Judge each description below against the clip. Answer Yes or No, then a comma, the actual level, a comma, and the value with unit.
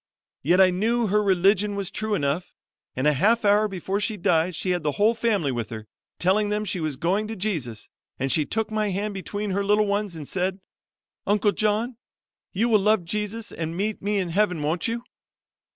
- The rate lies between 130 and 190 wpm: No, average, 200 wpm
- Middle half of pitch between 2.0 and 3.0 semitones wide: No, average, 3.6 semitones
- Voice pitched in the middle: No, high, 200 Hz